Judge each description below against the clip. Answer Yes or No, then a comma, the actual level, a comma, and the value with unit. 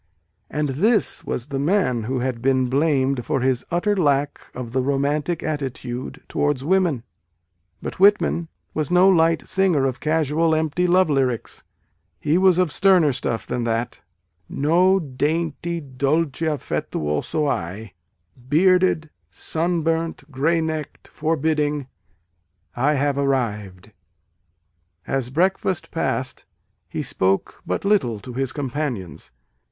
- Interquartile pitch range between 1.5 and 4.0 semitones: No, average, 4.4 semitones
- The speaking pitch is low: No, medium, 145 Hz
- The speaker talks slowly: Yes, slow, 130 wpm